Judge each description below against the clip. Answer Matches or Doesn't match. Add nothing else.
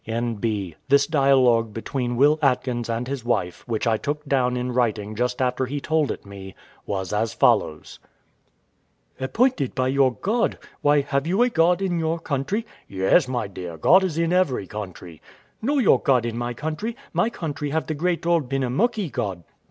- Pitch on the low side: Matches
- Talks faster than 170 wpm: Matches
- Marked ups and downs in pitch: Matches